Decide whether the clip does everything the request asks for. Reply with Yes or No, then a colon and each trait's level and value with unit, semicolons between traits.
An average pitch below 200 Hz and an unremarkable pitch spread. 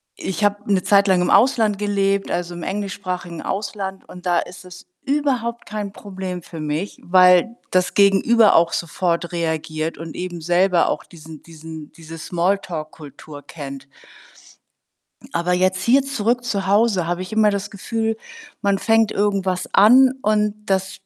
Yes: high, 190 Hz; average, 3.2 semitones